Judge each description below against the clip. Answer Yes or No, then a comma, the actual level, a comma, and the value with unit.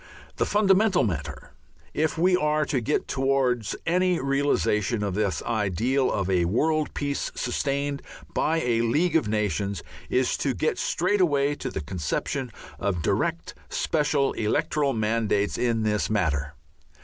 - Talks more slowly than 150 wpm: Yes, average, 140 wpm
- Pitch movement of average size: No, wide, 6.4 semitones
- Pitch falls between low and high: No, low, 130 Hz